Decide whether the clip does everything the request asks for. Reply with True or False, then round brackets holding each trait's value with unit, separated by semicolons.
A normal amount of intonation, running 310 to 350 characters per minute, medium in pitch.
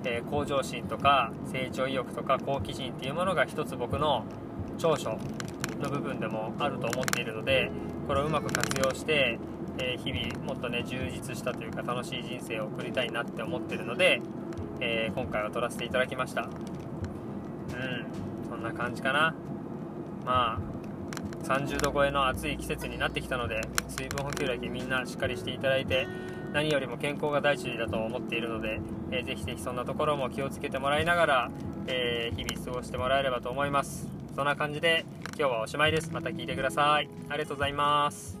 False (4.6 semitones; 385 characters per minute; 145 Hz)